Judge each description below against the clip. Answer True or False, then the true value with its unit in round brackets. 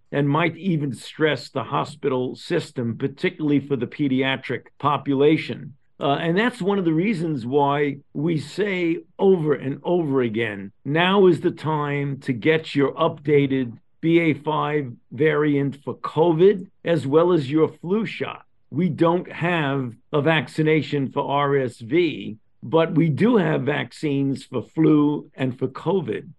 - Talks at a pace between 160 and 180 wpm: False (140 wpm)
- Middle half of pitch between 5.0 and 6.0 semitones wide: False (3.2 semitones)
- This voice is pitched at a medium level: True (150 Hz)